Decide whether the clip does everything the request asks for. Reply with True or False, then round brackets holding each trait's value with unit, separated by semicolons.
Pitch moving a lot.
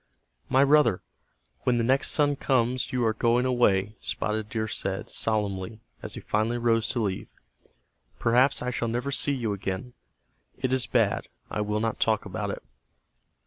False (2.9 semitones)